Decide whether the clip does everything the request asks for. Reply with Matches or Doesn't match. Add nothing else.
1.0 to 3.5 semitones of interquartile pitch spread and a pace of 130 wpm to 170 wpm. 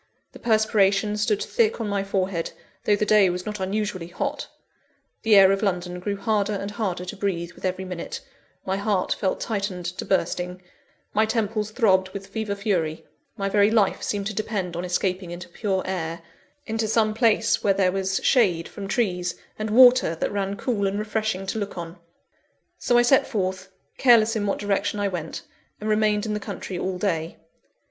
Doesn't match